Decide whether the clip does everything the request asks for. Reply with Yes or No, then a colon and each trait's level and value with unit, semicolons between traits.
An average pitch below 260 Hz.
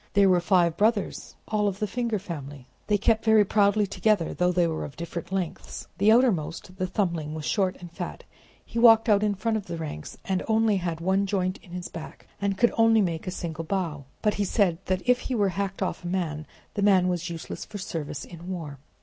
Yes: medium, 185 Hz